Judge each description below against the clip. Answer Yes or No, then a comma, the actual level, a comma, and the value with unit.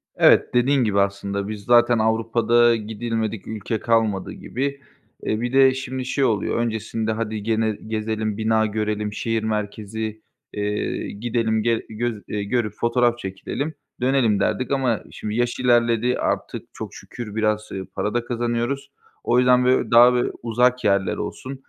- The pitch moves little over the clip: Yes, narrow, 2.3 semitones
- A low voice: Yes, low, 115 Hz